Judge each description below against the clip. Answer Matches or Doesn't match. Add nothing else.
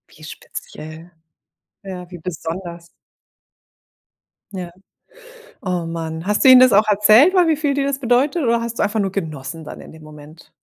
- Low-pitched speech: Doesn't match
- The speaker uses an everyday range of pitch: Doesn't match